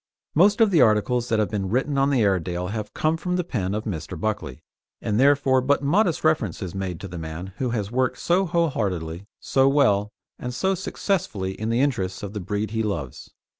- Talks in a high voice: No, low, 110 Hz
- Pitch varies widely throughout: Yes, wide, 6.7 semitones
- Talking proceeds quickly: Yes, fast, 210 wpm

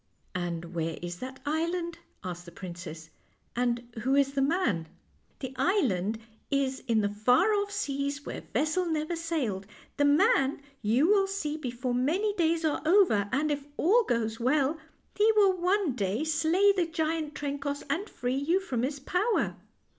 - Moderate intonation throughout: No, wide, 6.3 semitones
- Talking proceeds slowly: No, average, 170 wpm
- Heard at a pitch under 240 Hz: No, very high, 285 Hz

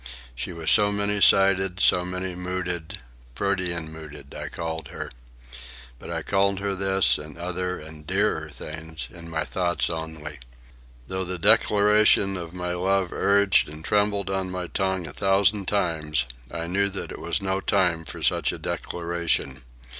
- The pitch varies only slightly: No, average, 3.2 semitones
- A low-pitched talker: Yes, very low, 90 Hz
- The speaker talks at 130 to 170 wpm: Yes, average, 155 wpm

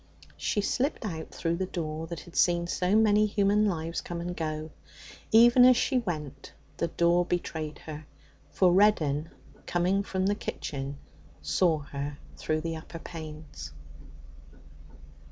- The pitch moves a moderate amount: Yes, average, 4.1 semitones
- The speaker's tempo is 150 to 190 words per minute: No, average, 140 wpm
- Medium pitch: Yes, medium, 170 Hz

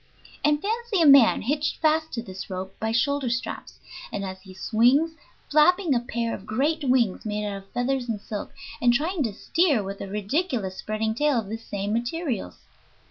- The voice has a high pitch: Yes, high, 240 Hz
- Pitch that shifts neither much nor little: No, wide, 6.1 semitones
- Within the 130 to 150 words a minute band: No, average, 185 wpm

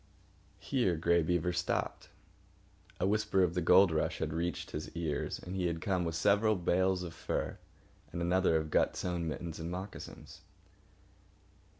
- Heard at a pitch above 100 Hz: No, very low, 90 Hz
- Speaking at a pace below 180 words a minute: Yes, average, 160 wpm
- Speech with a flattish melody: Yes, narrow, 2.3 semitones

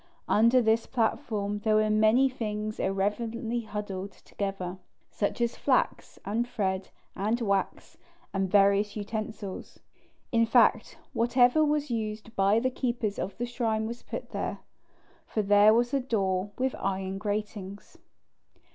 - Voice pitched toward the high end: Yes, high, 215 Hz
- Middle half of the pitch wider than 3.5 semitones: No, average, 2.7 semitones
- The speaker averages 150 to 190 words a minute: No, slow, 135 wpm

